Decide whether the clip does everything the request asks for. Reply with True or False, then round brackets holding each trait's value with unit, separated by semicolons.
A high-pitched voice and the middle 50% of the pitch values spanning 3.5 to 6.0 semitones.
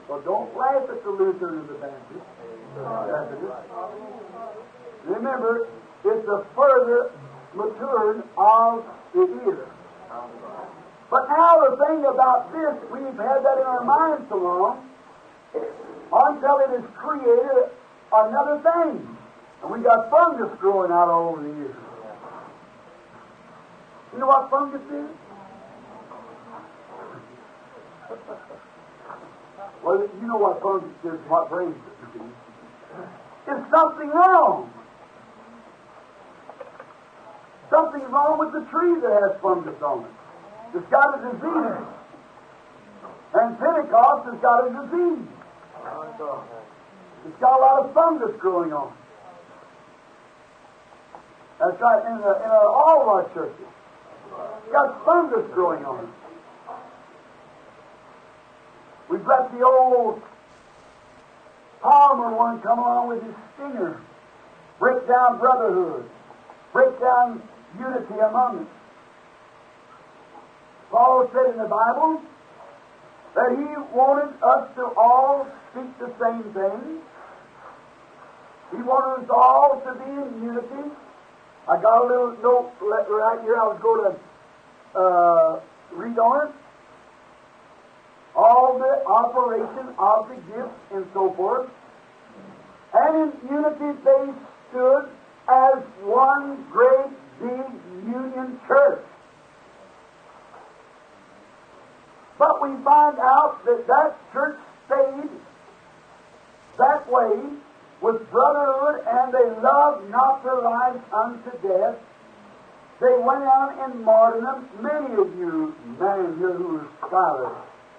True (265 Hz; 4.7 semitones)